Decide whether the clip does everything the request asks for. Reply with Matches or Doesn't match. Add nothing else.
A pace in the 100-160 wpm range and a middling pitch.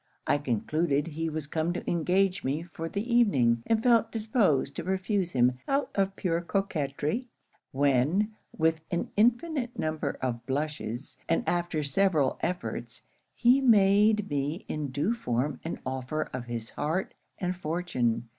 Matches